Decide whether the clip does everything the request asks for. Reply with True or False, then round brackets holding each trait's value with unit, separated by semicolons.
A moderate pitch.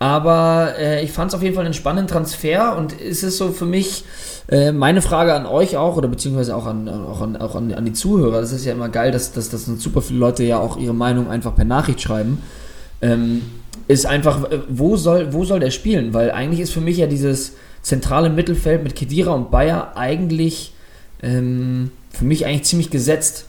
True (145 Hz)